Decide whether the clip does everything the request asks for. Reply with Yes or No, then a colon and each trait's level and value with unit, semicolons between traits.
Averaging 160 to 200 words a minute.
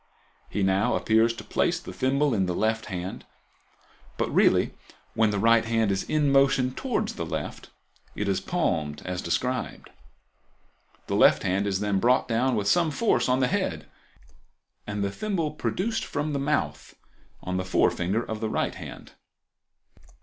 Yes: average, 165 wpm